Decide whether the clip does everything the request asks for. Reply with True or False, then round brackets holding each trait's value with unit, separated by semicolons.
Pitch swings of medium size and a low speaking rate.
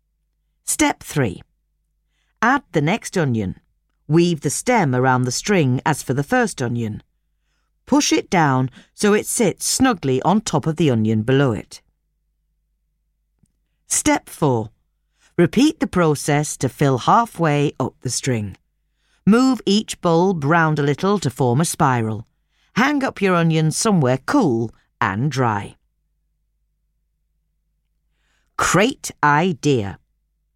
False (7.2 semitones; 120 wpm)